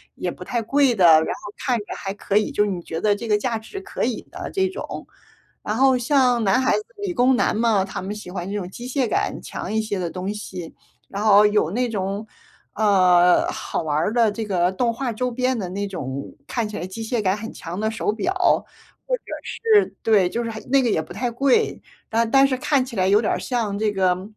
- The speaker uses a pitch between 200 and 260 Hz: Yes, high, 215 Hz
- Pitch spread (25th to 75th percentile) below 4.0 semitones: No, average, 4.4 semitones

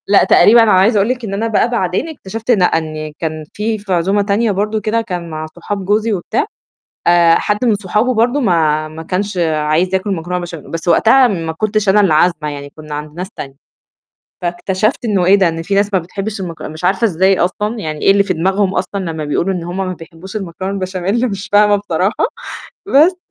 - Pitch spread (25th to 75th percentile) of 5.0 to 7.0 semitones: No, average, 3.8 semitones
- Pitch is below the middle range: No, high, 190 Hz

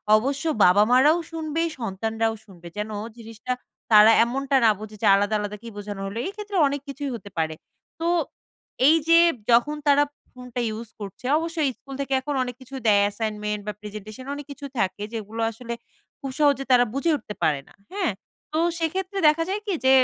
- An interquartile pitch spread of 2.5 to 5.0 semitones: No, wide, 5.5 semitones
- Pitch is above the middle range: Yes, high, 235 Hz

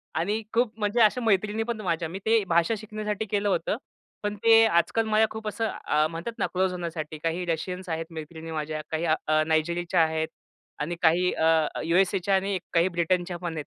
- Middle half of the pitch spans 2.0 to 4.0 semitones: No, average, 4.5 semitones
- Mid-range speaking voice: Yes, medium, 180 Hz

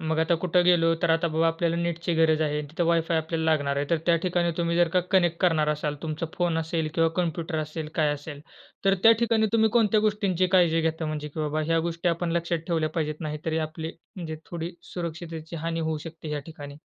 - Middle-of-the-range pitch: Yes, medium, 165 Hz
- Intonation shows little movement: Yes, narrow, 1.6 semitones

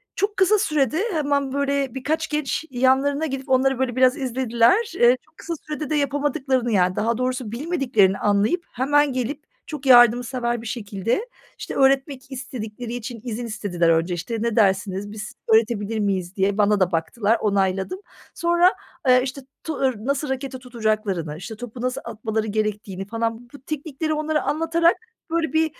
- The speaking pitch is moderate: No, very high, 250 Hz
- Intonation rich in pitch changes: No, average, 4.7 semitones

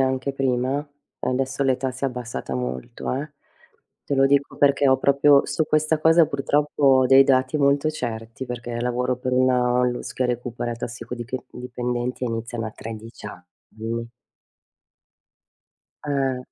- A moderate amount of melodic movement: No, narrow, 2.2 semitones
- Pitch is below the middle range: Yes, low, 130 Hz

